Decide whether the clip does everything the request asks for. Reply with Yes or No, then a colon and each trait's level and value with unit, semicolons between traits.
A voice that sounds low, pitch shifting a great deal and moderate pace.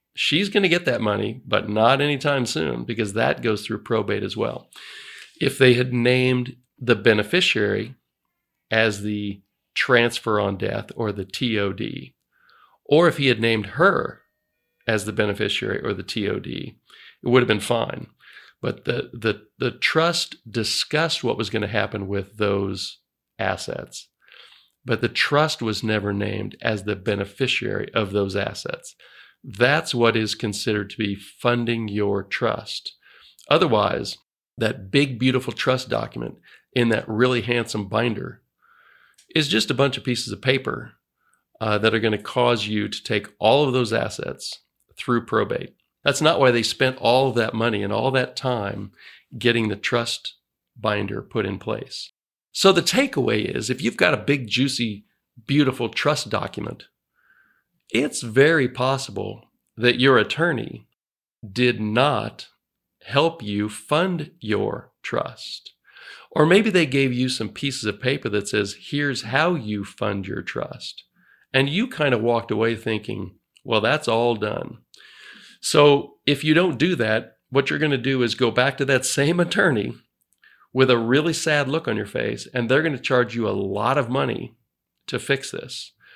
No: low, 120 Hz; average, 4.1 semitones; average, 160 wpm